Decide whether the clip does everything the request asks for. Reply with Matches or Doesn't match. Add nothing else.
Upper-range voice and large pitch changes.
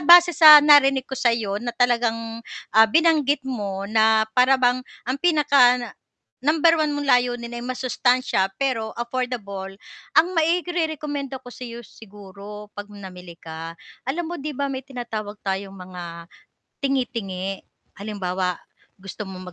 Matches